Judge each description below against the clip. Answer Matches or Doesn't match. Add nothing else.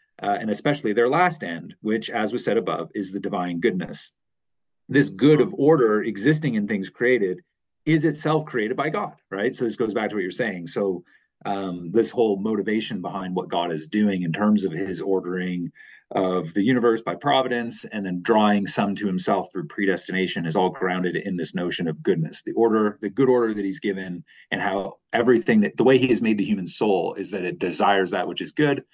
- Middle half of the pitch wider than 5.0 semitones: Matches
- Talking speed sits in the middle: Doesn't match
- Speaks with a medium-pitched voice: Doesn't match